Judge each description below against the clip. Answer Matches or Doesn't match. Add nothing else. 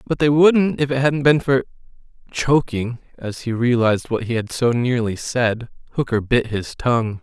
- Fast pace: Doesn't match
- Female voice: Doesn't match